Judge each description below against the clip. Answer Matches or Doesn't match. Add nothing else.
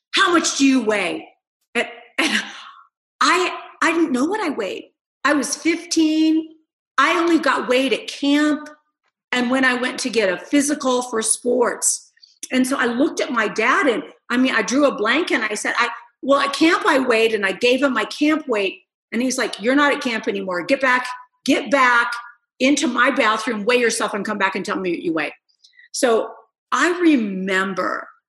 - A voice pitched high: Matches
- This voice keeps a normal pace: Matches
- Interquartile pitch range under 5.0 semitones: Matches